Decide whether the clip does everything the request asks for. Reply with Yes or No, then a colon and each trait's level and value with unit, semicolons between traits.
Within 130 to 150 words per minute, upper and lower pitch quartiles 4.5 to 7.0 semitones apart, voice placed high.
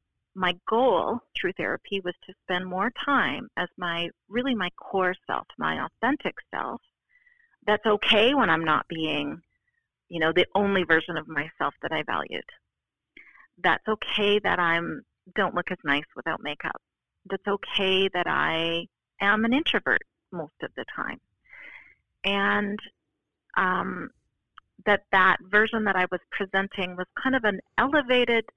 No: average, 145 wpm; average, 3.3 semitones; high, 195 Hz